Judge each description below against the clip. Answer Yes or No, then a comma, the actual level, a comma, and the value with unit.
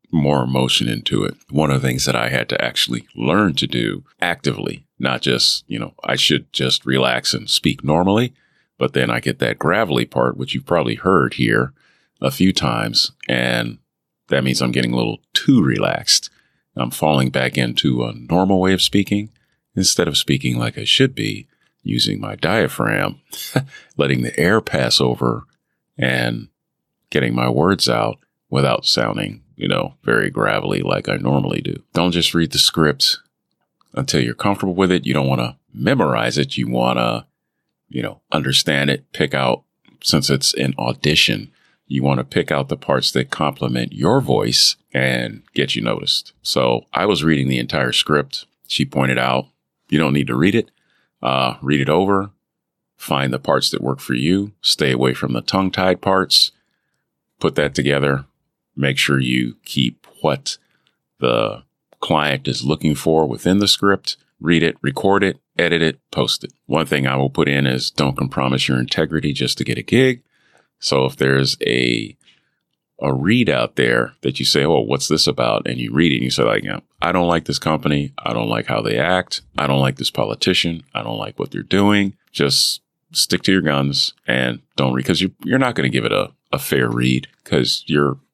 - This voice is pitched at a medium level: No, very low, 70 Hz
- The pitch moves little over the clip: No, average, 4.8 semitones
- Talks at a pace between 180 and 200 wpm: Yes, average, 185 wpm